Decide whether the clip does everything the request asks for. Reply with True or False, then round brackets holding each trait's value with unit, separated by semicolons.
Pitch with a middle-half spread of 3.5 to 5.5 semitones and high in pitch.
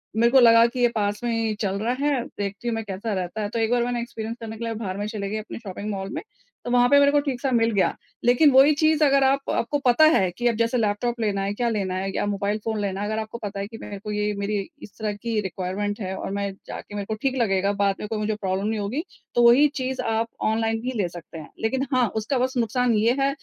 False (3.1 semitones; 220 Hz)